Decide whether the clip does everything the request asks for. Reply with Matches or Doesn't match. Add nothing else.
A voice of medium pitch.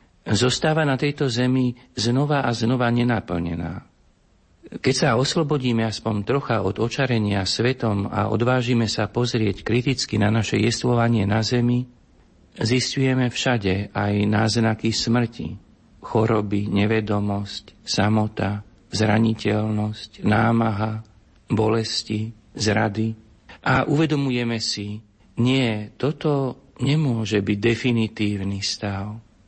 Doesn't match